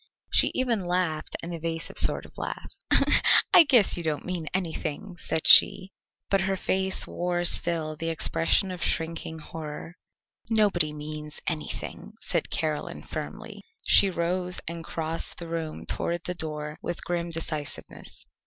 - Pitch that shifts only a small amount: Yes, narrow, 2.3 semitones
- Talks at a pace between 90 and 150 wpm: Yes, average, 145 wpm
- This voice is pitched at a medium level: Yes, medium, 170 Hz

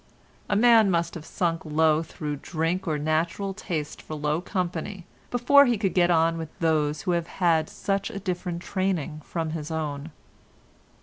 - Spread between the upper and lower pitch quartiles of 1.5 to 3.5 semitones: Yes, average, 3.2 semitones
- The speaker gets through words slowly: No, average, 170 wpm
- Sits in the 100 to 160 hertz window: No, medium, 170 Hz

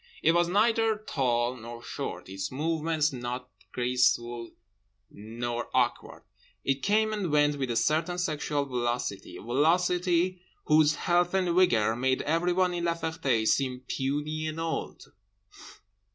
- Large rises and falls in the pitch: Yes, wide, 6.0 semitones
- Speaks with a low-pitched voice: No, medium, 150 Hz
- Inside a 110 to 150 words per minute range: Yes, slow, 135 wpm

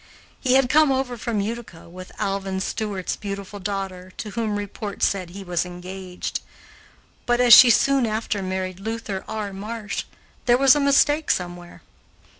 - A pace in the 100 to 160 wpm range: Yes, average, 155 wpm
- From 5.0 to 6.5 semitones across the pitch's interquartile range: No, average, 4.0 semitones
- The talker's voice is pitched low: No, high, 205 Hz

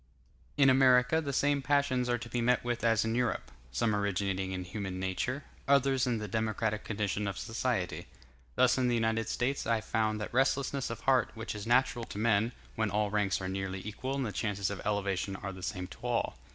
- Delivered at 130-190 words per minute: No, fast, 205 wpm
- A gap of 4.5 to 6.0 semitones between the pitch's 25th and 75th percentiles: No, average, 3.8 semitones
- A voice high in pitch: No, low, 115 Hz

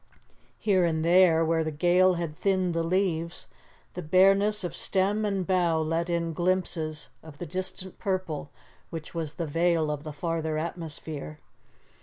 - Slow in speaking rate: No, average, 155 wpm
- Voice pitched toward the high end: No, medium, 170 Hz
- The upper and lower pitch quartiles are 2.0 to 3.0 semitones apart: Yes, narrow, 2.6 semitones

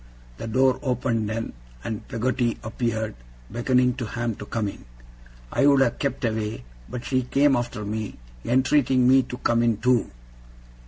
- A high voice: No, low, 120 Hz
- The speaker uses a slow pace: No, average, 160 wpm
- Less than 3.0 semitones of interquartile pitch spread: Yes, narrow, 2.6 semitones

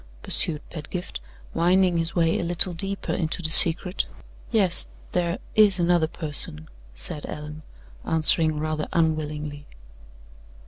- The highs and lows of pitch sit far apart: No, narrow, 2.5 semitones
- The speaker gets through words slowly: Yes, slow, 120 wpm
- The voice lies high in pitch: No, medium, 165 Hz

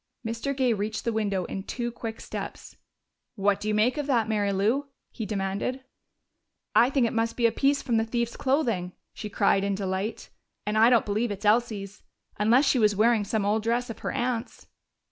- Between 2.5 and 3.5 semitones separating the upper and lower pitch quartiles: Yes, average, 2.8 semitones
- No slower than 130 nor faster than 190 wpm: No, average, 200 wpm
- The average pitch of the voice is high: Yes, high, 225 Hz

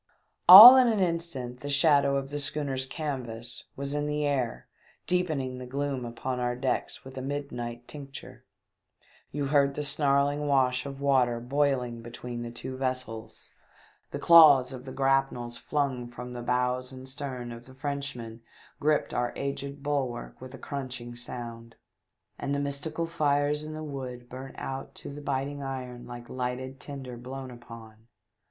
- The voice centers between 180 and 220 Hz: No, low, 135 Hz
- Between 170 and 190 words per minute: No, average, 160 wpm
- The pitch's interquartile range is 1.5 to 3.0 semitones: Yes, narrow, 2.5 semitones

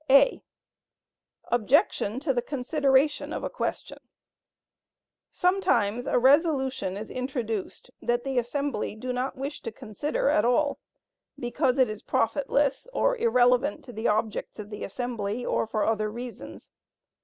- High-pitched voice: Yes, very high, 250 Hz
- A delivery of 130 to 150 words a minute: Yes, slow, 135 wpm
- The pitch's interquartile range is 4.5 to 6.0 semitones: No, average, 4.0 semitones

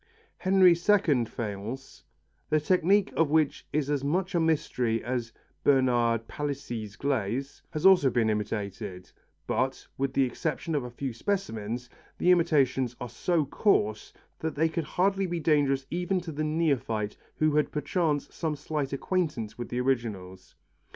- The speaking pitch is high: No, medium, 140 Hz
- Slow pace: No, average, 145 wpm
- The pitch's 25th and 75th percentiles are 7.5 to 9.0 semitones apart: No, wide, 5.4 semitones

